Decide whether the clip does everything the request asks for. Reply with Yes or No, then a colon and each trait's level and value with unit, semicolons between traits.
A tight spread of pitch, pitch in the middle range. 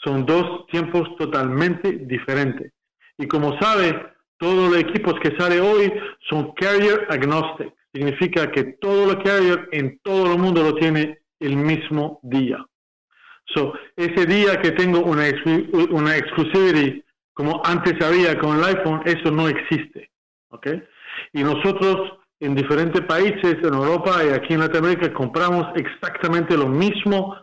No: average, 3.1 semitones; medium, 165 Hz